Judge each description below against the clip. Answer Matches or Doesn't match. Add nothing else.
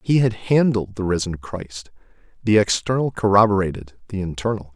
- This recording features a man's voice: Matches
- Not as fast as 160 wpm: Matches